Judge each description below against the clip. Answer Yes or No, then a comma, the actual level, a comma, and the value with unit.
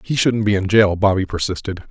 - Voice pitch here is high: No, low, 100 Hz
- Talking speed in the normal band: No, fast, 220 wpm